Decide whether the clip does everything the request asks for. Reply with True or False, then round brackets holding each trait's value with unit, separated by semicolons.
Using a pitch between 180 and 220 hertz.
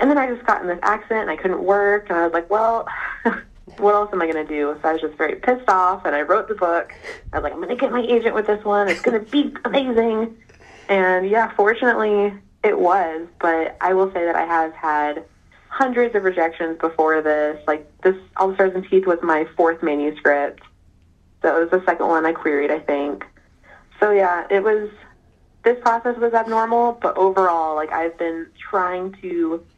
True (185 Hz)